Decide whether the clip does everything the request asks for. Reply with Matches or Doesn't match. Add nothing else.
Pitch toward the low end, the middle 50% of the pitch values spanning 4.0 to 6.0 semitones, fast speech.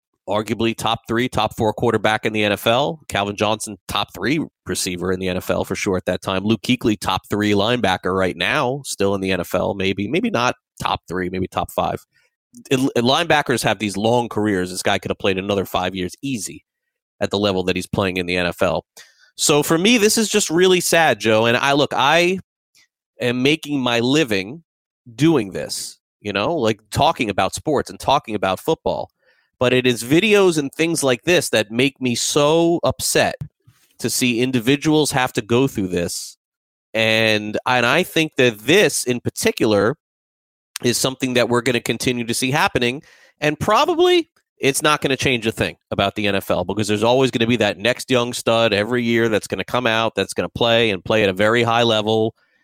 Doesn't match